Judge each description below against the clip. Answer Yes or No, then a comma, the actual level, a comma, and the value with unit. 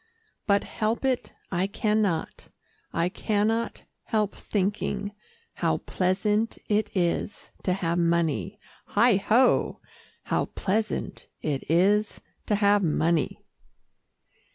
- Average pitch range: Yes, average, 3.2 semitones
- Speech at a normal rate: No, slow, 110 wpm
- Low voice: No, high, 205 Hz